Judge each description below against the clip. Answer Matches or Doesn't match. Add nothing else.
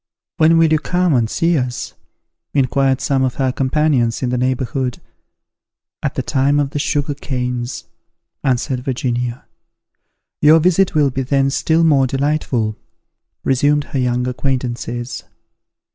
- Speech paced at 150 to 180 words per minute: Doesn't match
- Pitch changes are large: Doesn't match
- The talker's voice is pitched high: Doesn't match